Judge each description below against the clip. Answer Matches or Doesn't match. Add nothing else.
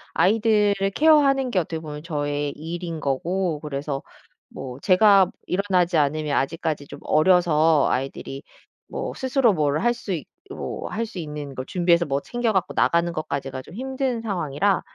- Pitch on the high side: Doesn't match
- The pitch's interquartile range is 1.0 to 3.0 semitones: Doesn't match